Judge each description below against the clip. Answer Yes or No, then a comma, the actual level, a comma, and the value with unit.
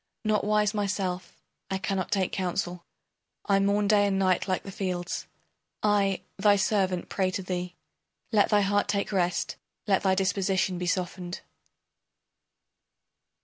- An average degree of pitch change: No, narrow, 1.8 semitones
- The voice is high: Yes, high, 195 Hz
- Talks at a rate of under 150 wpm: Yes, average, 140 wpm